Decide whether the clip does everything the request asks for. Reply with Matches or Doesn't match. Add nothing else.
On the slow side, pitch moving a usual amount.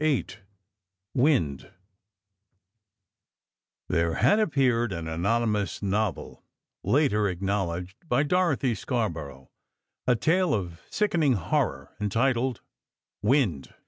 Doesn't match